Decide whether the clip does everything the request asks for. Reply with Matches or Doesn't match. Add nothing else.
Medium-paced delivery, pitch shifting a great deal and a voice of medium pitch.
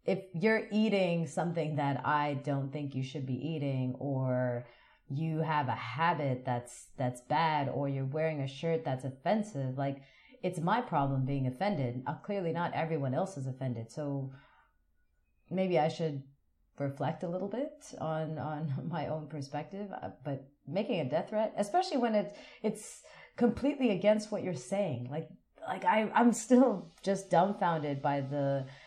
Matches